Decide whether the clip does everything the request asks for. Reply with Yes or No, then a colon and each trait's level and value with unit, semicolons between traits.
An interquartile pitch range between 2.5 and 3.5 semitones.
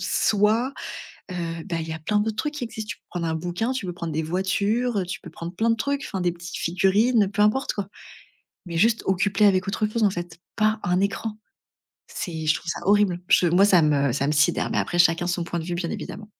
No: average, 3.9 semitones